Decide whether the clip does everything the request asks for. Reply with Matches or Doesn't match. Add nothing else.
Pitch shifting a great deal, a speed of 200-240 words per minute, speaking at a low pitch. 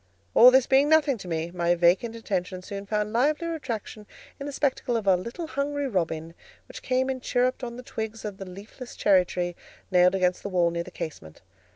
Doesn't match